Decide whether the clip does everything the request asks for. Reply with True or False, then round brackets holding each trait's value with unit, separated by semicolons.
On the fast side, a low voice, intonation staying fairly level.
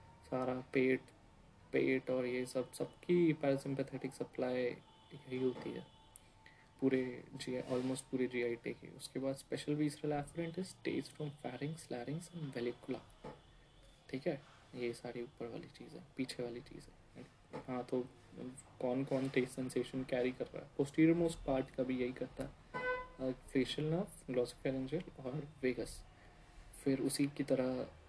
False (145 wpm; 130 Hz; 2.3 semitones)